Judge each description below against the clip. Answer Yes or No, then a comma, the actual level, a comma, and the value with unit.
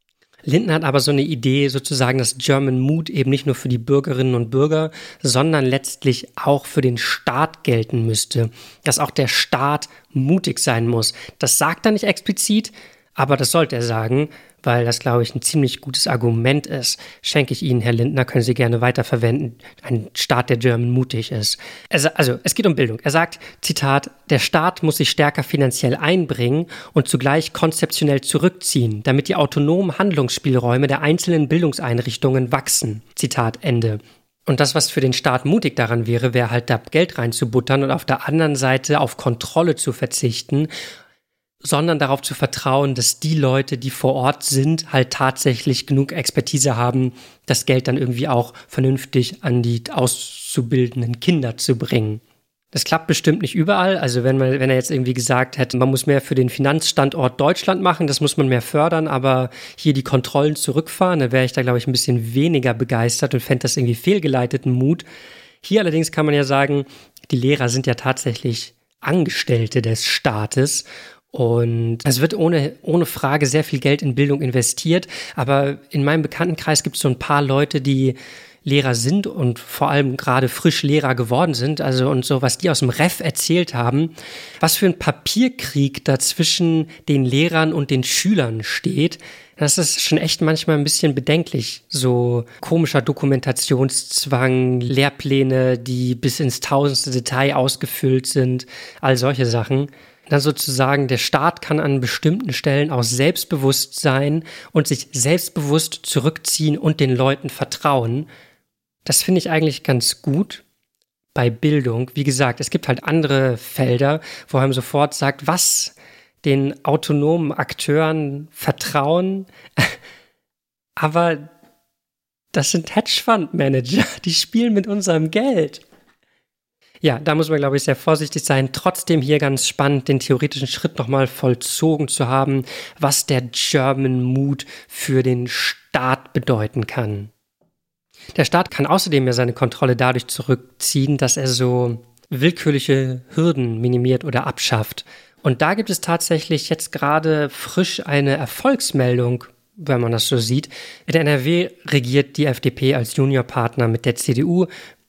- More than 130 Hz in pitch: Yes, medium, 140 Hz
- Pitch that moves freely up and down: No, average, 3.6 semitones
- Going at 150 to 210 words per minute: Yes, average, 160 wpm